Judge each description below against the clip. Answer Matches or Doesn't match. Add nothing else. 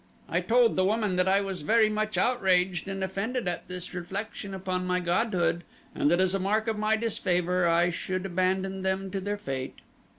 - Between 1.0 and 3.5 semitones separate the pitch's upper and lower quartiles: Matches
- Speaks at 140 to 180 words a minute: Doesn't match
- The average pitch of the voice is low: Doesn't match